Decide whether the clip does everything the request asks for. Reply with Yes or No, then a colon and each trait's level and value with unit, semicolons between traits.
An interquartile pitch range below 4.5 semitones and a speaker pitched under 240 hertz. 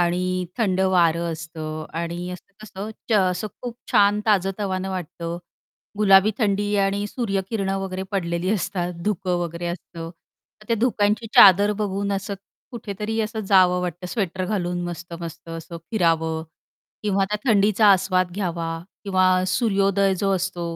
Yes: average, 2.8 semitones; high, 190 Hz